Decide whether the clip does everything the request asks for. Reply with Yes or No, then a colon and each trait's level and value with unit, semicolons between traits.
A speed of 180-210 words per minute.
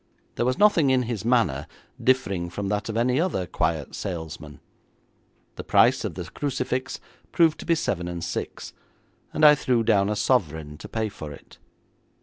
No: average, 170 wpm